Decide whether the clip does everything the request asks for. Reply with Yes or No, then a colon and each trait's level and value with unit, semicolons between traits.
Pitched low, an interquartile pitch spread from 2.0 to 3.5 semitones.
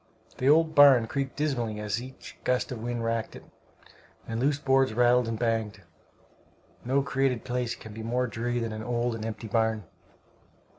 Yes: low, 120 Hz; average, 2.7 semitones